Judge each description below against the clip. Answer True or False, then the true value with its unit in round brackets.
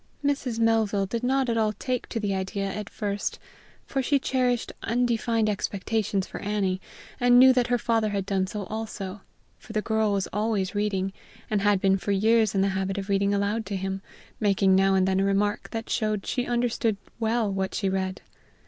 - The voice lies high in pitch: True (210 Hz)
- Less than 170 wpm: False (195 wpm)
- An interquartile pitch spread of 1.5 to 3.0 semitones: True (2.7 semitones)